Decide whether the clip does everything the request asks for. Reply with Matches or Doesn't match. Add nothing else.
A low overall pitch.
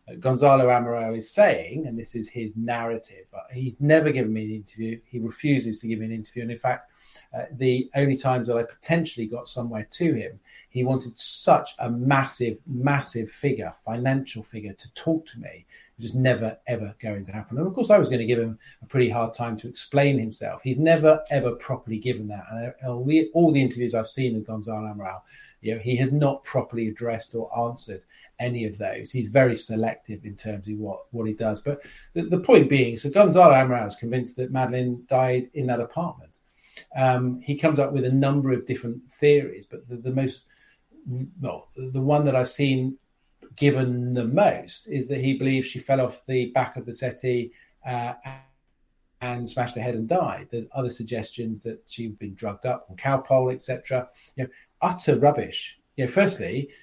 Matches